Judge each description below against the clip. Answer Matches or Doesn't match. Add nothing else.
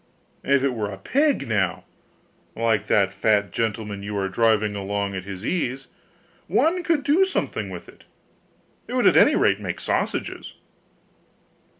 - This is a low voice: Matches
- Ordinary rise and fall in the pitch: Doesn't match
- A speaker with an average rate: Matches